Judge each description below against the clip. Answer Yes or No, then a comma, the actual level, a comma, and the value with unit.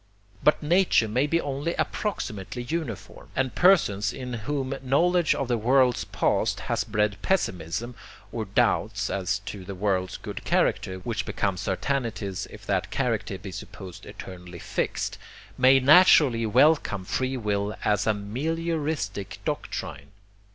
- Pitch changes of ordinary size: No, wide, 5.9 semitones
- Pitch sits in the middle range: No, low, 115 Hz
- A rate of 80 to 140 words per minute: Yes, slow, 135 wpm